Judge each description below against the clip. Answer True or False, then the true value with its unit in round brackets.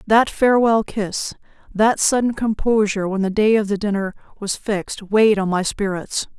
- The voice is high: True (210 Hz)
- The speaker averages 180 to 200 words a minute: False (170 wpm)